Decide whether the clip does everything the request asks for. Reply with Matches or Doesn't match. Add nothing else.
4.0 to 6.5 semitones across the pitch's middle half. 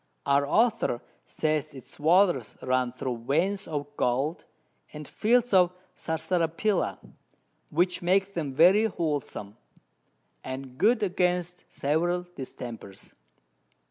Matches